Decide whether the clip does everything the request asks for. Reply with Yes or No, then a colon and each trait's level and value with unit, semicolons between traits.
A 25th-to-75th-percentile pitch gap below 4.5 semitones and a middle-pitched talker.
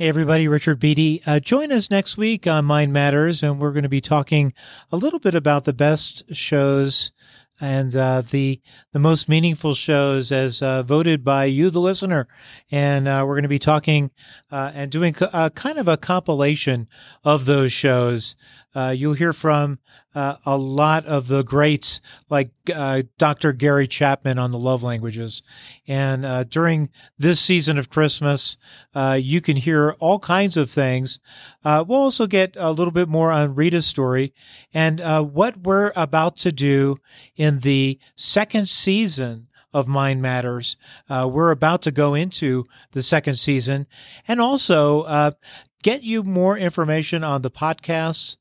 Yes: average, 3.1 semitones; medium, 150 Hz